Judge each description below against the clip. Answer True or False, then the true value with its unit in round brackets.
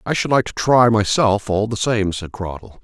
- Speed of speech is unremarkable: False (235 wpm)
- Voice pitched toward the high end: False (105 Hz)